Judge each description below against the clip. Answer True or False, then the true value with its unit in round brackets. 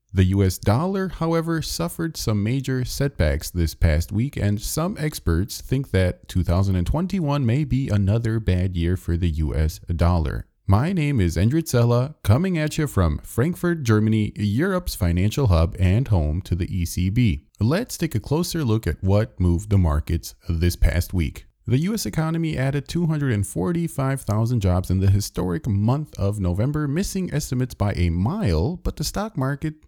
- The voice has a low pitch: True (105 Hz)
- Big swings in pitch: True (8.0 semitones)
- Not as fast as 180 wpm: True (160 wpm)